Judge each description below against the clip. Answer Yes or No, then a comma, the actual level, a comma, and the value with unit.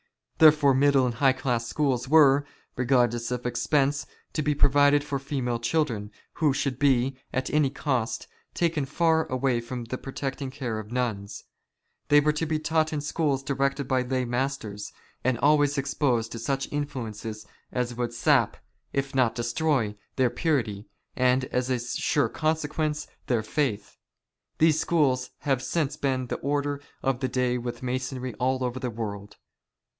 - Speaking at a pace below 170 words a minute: Yes, average, 160 wpm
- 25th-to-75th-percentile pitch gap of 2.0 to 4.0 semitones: Yes, average, 2.9 semitones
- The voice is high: No, low, 130 Hz